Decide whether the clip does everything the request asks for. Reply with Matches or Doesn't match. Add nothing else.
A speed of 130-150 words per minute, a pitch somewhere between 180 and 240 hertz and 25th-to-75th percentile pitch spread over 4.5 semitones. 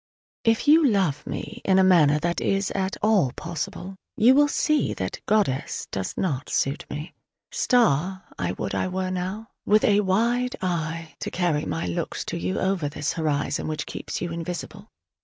Doesn't match